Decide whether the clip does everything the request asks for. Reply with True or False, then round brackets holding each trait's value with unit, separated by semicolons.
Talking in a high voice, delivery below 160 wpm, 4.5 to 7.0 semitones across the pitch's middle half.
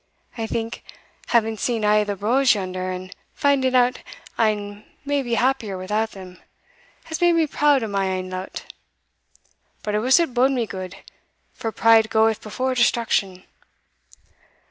False (220 Hz; 150 wpm; 4.1 semitones)